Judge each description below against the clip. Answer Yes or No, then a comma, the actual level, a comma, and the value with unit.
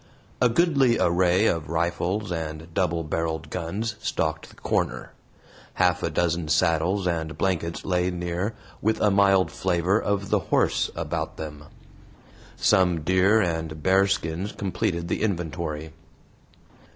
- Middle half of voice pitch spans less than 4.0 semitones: Yes, average, 3.1 semitones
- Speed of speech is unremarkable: No, slow, 130 wpm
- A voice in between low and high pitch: No, very low, 90 Hz